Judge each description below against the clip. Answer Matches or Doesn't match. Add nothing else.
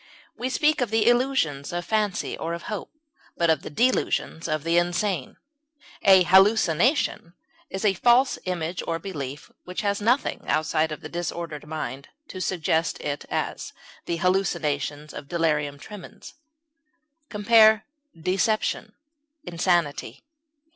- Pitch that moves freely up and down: Doesn't match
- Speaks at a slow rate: Matches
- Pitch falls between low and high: Matches